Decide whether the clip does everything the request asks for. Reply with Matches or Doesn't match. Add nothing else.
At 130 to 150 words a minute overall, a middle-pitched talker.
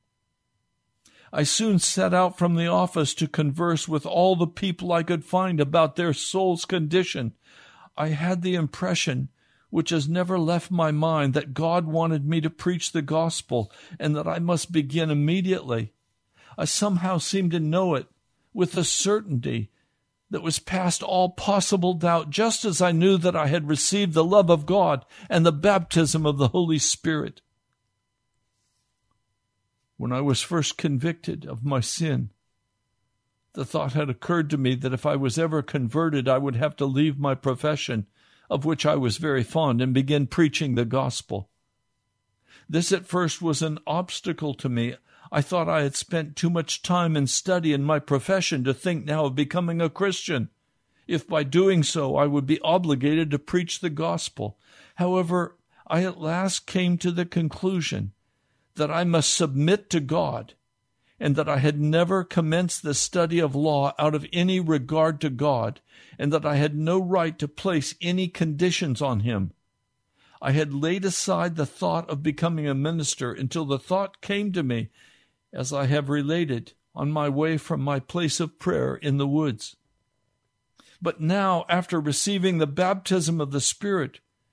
Doesn't match